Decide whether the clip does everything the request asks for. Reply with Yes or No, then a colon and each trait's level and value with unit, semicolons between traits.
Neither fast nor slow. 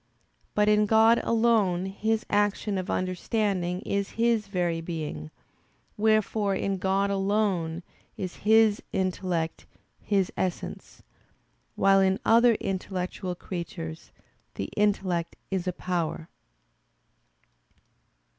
No: slow, 100 wpm